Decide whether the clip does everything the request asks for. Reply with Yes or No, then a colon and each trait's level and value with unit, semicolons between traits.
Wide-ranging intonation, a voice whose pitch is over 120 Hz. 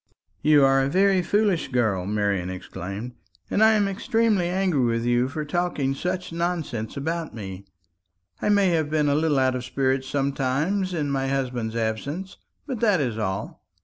Yes: wide, 6.7 semitones; medium, 140 Hz